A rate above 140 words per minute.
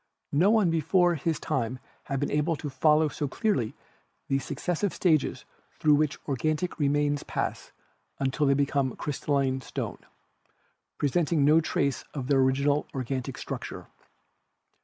No: slow, 135 wpm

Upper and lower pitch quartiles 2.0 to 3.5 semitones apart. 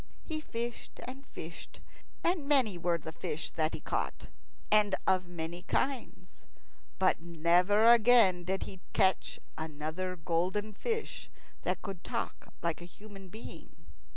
No: average, 4.7 semitones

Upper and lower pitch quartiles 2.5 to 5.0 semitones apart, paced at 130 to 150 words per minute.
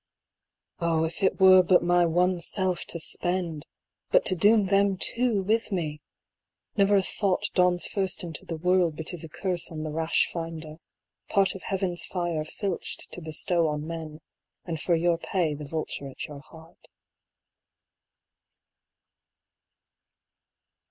Yes: average, 2.8 semitones; average, 145 wpm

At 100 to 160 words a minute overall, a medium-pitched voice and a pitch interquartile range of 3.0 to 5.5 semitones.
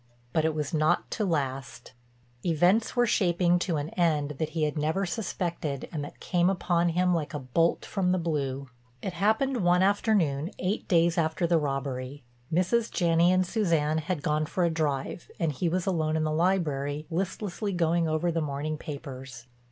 No: average, 175 wpm; medium, 165 Hz; average, 3.4 semitones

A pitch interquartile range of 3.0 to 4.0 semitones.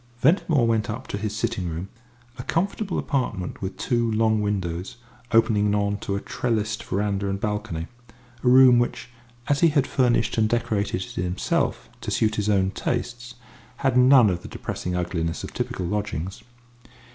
Yes: average, 3.7 semitones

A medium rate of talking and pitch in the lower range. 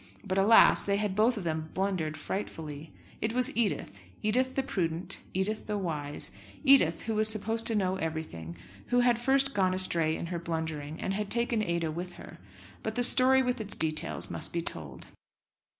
No: average, 180 wpm; high, 190 Hz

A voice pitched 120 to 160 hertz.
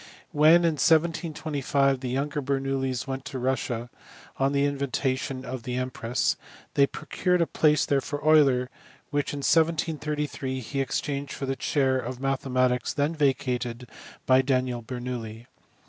Yes: low, 135 Hz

